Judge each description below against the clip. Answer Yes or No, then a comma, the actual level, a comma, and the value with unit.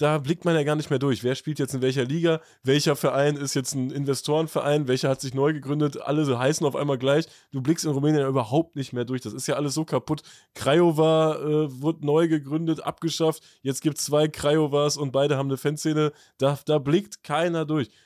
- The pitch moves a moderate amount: No, narrow, 2.2 semitones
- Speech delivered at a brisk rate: Yes, fast, 225 wpm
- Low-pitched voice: No, medium, 145 Hz